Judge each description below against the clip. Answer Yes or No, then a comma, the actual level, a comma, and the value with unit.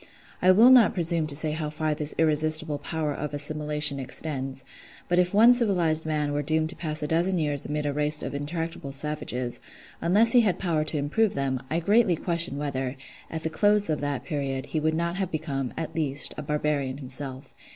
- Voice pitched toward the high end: No, medium, 155 Hz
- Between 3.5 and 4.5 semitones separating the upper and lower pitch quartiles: No, average, 2.8 semitones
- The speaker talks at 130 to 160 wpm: No, average, 200 wpm